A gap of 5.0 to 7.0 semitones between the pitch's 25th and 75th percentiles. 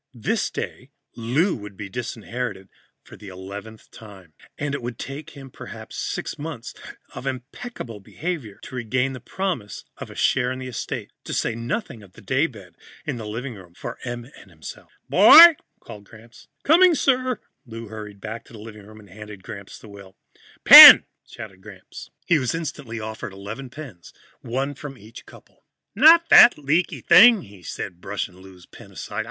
Yes: average, 5.3 semitones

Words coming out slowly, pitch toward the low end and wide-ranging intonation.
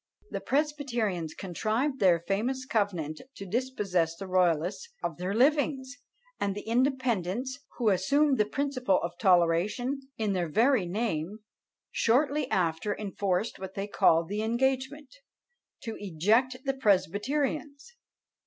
No: slow, 125 wpm; high, 215 Hz; wide, 6.2 semitones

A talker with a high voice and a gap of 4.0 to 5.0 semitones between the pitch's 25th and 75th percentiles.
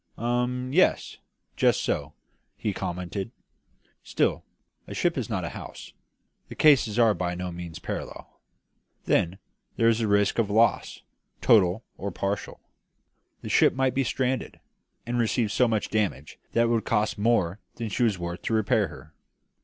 No: low, 110 Hz; average, 4.4 semitones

